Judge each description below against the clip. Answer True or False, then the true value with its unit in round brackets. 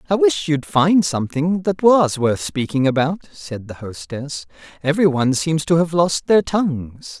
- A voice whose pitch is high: False (150 Hz)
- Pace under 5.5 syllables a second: True (4.6 syllables/s)